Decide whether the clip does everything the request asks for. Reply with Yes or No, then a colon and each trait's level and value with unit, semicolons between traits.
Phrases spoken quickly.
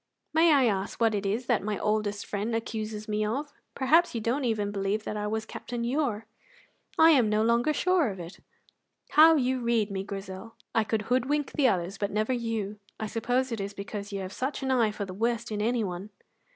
Yes: fast, 210 wpm